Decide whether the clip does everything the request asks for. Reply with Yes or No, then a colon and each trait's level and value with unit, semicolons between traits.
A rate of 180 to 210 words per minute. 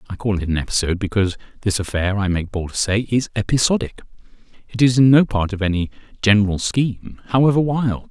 Yes: average, 185 wpm